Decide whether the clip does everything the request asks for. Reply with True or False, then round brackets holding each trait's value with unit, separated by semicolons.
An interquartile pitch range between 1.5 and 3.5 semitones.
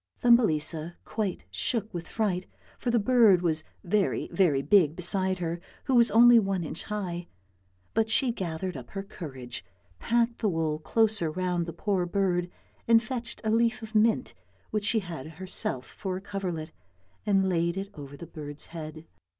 False (4.8 semitones)